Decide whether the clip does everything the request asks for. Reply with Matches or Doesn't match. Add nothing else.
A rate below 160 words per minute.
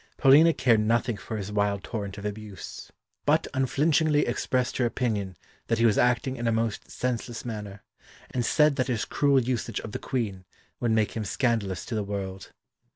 Doesn't match